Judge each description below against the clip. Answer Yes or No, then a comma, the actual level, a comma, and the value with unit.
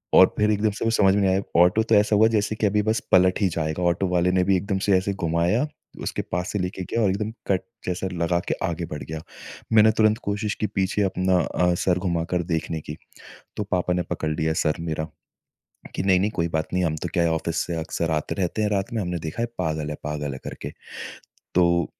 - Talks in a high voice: No, very low, 90 Hz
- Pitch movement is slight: No, average, 3.3 semitones